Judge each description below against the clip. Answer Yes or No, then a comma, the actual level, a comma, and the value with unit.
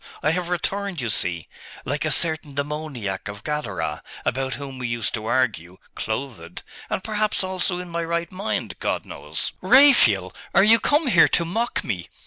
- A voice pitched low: No, medium, 150 Hz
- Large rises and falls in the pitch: Yes, wide, 8.2 semitones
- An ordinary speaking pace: Yes, average, 170 wpm